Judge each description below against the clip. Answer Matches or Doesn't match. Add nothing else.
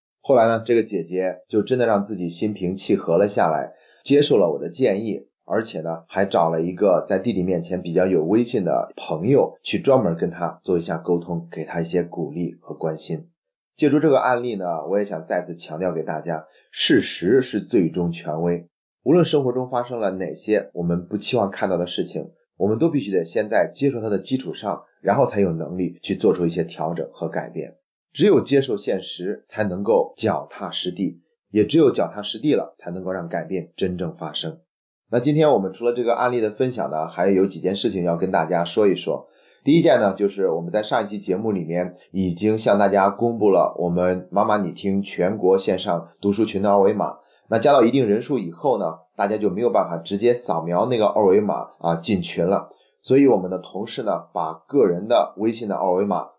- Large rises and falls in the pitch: Doesn't match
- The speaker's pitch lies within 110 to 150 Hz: Doesn't match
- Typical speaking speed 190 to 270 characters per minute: Doesn't match